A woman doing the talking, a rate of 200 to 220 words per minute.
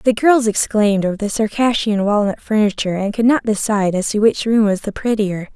Yes: female; fast, 205 wpm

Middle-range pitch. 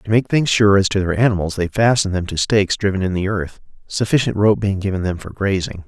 No: low, 100 Hz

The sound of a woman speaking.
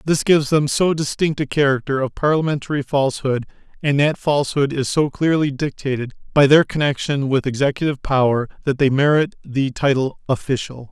No: male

